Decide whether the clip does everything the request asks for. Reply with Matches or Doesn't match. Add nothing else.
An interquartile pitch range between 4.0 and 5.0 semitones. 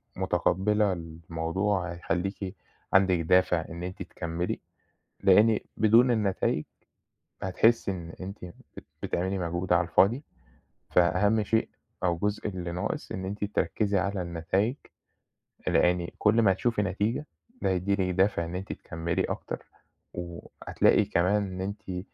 Doesn't match